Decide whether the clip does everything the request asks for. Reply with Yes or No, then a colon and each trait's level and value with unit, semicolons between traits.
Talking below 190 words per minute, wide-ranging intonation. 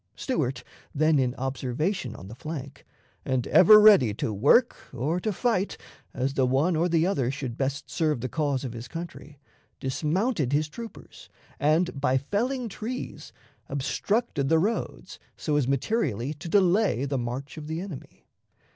Yes: average, 155 wpm; wide, 5.8 semitones